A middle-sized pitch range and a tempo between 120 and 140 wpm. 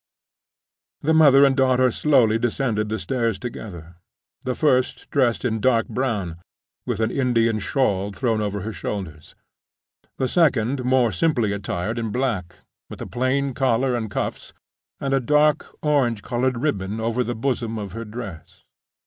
No: average, 3.6 semitones; average, 150 wpm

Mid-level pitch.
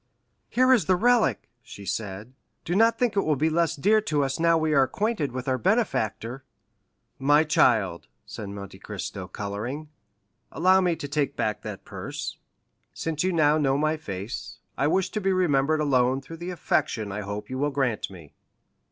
Yes: medium, 145 Hz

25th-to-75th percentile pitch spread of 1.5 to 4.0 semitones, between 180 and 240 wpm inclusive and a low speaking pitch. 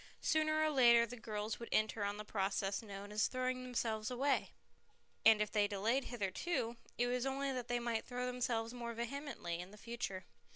No: average, 3.1 semitones; average, 195 wpm; high, 235 Hz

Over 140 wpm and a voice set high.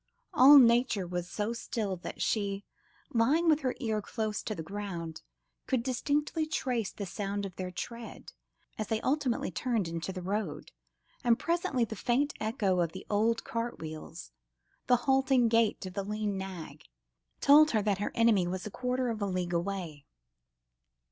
Yes: average, 170 wpm; high, 215 Hz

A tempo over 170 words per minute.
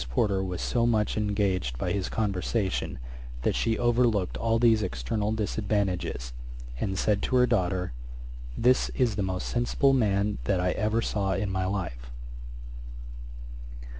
No: average, 140 wpm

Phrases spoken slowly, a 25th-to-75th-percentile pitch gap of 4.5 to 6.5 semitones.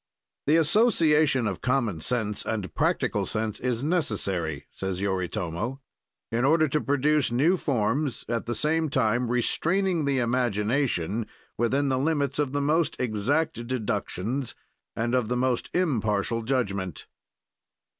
Yes: slow, 130 wpm; average, 5.2 semitones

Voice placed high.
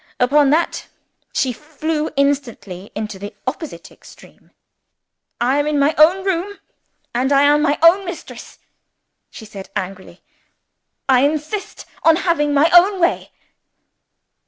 Yes: very high, 290 Hz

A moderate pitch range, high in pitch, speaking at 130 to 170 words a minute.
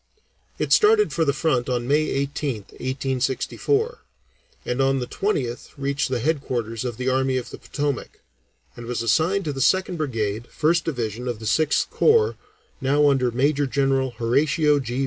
No: average, 3.6 semitones; low, 135 Hz; average, 165 wpm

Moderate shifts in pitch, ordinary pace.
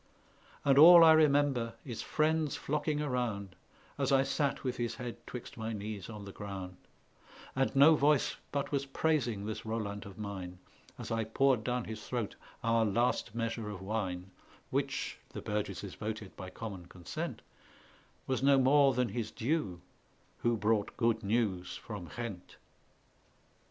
Yes: average, 4.9 semitones; average, 150 wpm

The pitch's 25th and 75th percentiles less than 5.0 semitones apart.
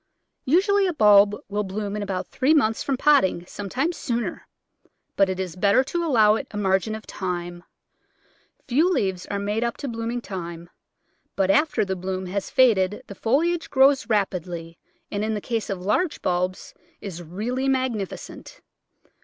No: wide, 5.4 semitones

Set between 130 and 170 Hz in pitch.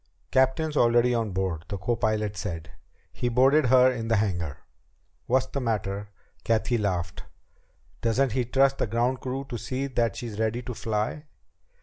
No: low, 115 Hz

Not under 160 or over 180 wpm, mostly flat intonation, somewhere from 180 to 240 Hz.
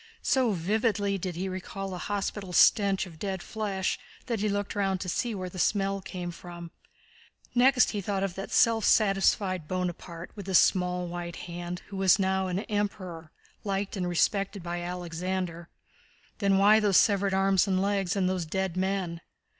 Yes: average, 170 wpm; narrow, 2.1 semitones; high, 190 Hz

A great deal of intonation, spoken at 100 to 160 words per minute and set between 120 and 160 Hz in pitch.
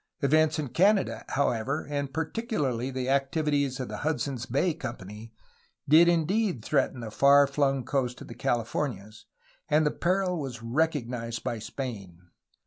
No: average, 4.5 semitones; average, 140 wpm; medium, 140 Hz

